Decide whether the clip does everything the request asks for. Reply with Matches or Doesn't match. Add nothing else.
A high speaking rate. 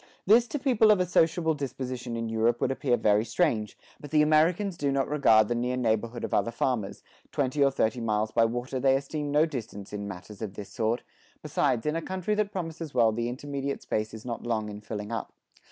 Matches